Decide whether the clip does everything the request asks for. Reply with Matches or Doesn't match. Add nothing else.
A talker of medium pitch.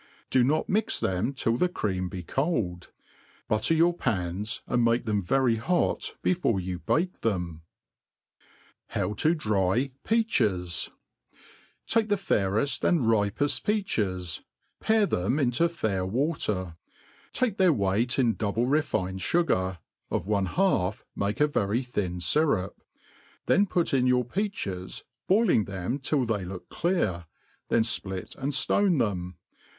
Doesn't match